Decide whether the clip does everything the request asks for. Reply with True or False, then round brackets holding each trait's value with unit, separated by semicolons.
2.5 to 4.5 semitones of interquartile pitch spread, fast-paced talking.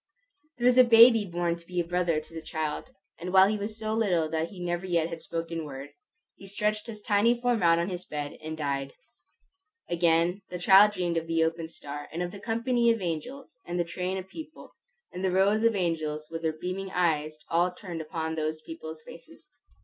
True (3.9 semitones; 210 wpm)